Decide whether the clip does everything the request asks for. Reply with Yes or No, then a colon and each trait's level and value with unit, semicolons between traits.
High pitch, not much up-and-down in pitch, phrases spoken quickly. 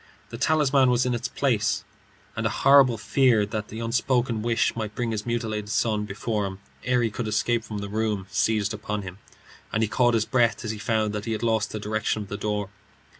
No: low, 110 Hz; narrow, 2.2 semitones; fast, 220 wpm